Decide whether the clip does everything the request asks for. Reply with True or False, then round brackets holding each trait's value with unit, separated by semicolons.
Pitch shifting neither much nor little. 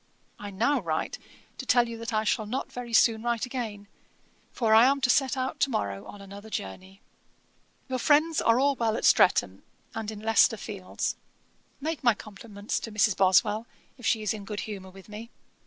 True (3.3 semitones)